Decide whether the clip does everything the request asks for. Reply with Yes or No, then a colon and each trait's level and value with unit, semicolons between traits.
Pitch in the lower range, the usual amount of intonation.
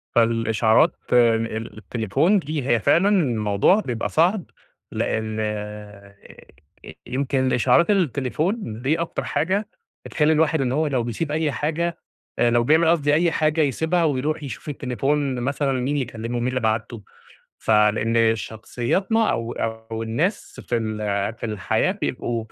No: low, 130 Hz; wide, 5.7 semitones